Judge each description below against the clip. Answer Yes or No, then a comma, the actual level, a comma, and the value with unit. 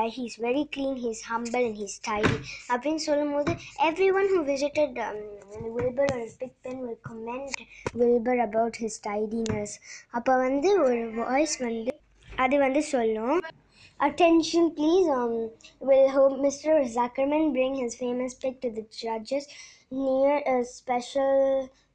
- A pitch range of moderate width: Yes, average, 3.3 semitones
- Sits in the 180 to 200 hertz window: No, very high, 260 Hz